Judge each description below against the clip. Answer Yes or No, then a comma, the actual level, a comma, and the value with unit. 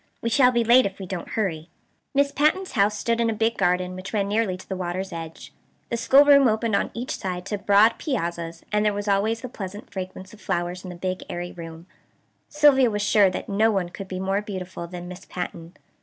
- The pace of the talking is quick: Yes, fast, 220 wpm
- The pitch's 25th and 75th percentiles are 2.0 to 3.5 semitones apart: No, average, 3.9 semitones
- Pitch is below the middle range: No, high, 200 Hz